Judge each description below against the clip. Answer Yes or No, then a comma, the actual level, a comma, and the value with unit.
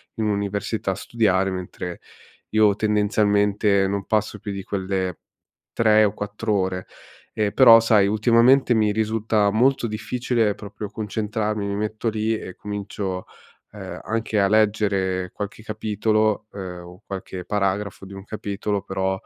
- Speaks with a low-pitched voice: Yes, low, 105 Hz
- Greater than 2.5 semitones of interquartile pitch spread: No, narrow, 1.8 semitones